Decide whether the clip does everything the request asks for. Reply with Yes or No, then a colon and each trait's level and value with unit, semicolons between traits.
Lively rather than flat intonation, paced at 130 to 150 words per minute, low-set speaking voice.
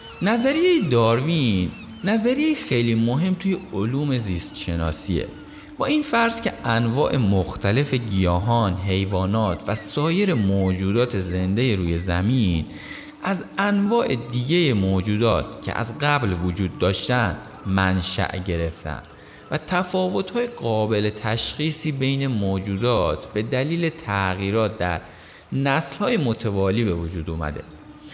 No: wide, 7.9 semitones; slow, 105 wpm; low, 110 Hz